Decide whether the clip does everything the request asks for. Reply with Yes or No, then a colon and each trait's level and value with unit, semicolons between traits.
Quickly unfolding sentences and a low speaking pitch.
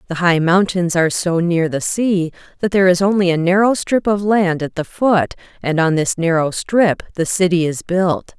No: fast, 210 wpm; medium, 180 Hz